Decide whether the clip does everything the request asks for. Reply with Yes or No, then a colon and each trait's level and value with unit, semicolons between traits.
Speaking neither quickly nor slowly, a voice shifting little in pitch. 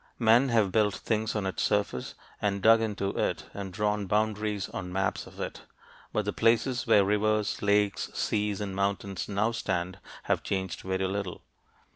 Yes: average, 165 wpm; narrow, 1.9 semitones